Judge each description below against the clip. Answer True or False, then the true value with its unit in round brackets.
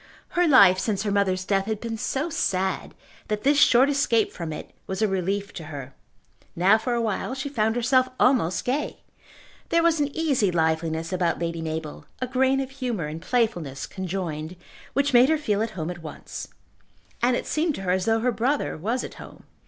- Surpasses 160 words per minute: True (195 wpm)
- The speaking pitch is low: False (215 Hz)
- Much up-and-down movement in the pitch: True (6.6 semitones)